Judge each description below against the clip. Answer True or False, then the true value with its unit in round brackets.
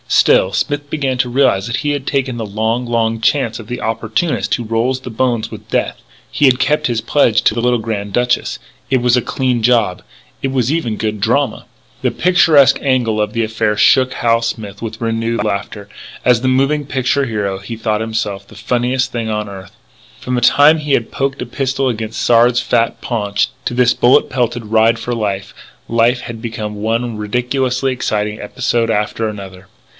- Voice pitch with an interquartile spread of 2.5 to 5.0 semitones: True (2.9 semitones)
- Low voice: True (115 Hz)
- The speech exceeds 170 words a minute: True (190 wpm)